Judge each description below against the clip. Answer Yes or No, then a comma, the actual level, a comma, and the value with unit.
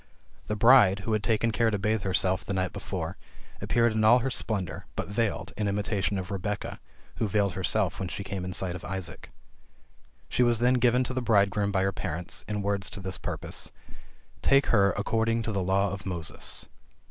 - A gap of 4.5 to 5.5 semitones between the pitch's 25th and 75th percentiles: No, average, 2.8 semitones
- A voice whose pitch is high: No, low, 100 Hz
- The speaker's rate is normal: Yes, average, 195 wpm